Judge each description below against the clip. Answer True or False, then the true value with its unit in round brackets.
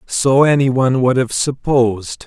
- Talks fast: False (160 wpm)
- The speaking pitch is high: False (130 Hz)